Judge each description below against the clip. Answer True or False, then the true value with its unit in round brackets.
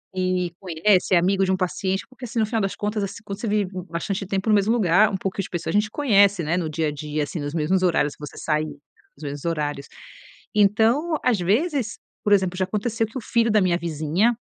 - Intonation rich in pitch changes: False (3.9 semitones)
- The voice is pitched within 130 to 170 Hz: False (190 Hz)